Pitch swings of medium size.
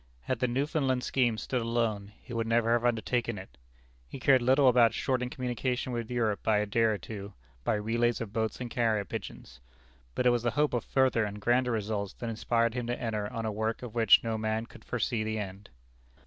No: narrow, 2.2 semitones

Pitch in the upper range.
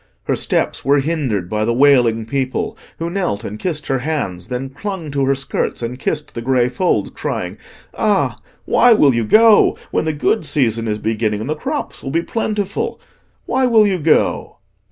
No: medium, 140 Hz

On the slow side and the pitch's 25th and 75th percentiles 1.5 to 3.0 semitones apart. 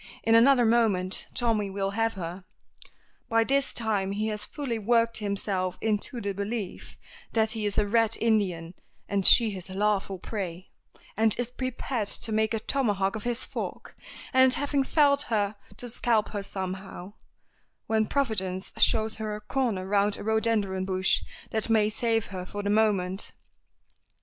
No: average, 160 wpm; average, 2.7 semitones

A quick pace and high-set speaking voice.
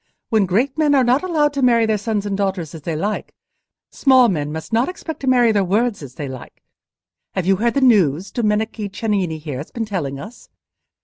Yes: fast, 210 wpm; high, 210 Hz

